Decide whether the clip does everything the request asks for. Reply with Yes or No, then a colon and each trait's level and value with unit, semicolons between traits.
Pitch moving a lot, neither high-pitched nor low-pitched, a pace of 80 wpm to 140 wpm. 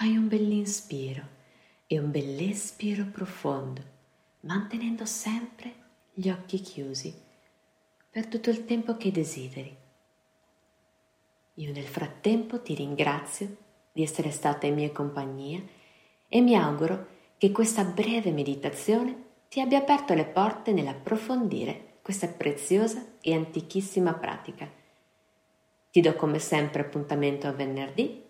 Yes: wide, 7.0 semitones; medium, 180 Hz; slow, 115 wpm